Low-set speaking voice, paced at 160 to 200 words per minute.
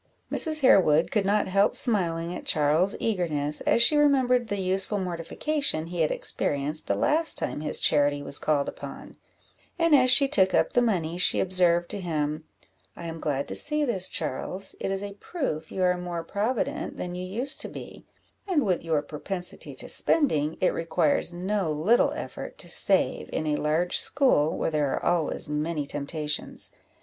No: medium, 180 Hz; average, 180 wpm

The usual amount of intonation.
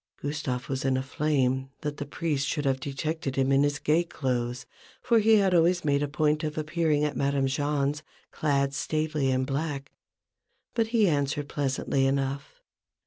No: narrow, 2.3 semitones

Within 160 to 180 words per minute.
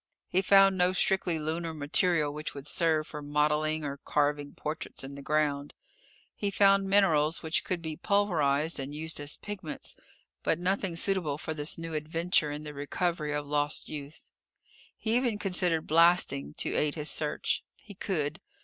Yes: average, 165 wpm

